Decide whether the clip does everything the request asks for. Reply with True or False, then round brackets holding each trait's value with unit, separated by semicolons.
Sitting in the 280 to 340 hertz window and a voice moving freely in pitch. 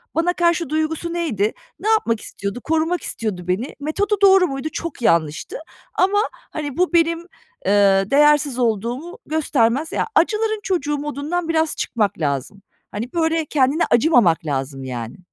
True (295 Hz; 7.3 semitones)